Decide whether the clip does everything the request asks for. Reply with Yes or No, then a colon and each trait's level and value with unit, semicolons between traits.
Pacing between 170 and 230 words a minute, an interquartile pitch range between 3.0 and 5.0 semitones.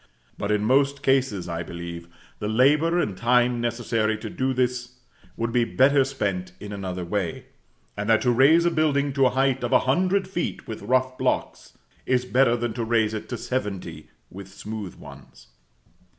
Yes: average, 180 wpm; average, 4.2 semitones